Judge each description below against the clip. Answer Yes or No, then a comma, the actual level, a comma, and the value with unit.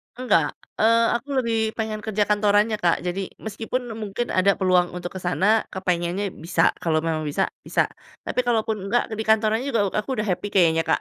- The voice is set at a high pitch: Yes, high, 205 Hz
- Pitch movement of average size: Yes, average, 3.6 semitones